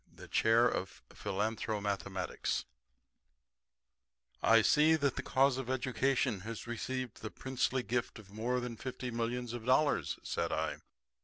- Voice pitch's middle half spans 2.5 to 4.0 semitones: Yes, average, 2.9 semitones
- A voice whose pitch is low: Yes, low, 120 Hz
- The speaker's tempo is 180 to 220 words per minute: No, slow, 135 wpm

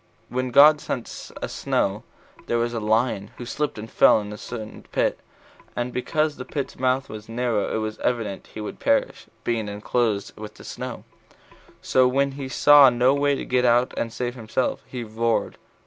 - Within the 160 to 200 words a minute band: Yes, average, 185 wpm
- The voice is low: Yes, low, 120 Hz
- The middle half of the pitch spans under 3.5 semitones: Yes, average, 2.9 semitones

